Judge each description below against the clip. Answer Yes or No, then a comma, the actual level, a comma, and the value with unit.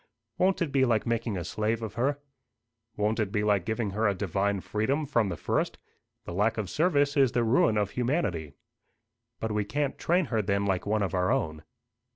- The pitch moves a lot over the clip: No, average, 4.2 semitones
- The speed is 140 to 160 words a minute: No, average, 200 wpm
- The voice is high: No, low, 110 Hz